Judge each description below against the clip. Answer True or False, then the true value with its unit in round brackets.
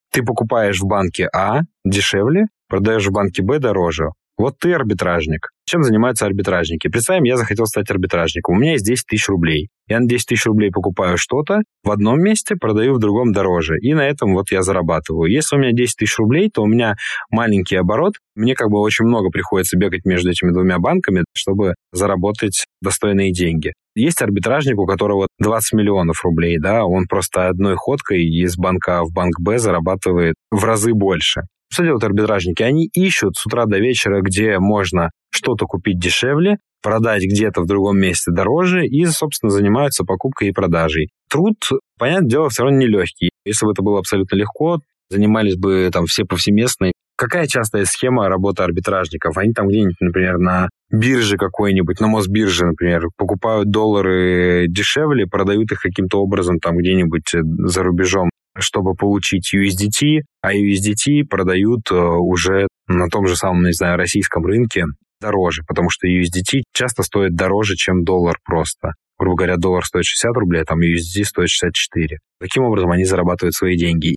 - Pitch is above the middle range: False (100 Hz)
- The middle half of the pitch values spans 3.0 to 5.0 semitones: True (3.3 semitones)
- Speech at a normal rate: False (165 wpm)